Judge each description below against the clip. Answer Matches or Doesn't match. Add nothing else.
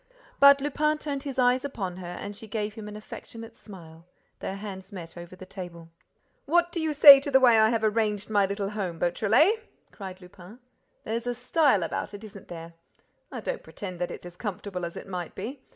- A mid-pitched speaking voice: Doesn't match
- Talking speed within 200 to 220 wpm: Matches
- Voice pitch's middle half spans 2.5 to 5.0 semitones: Doesn't match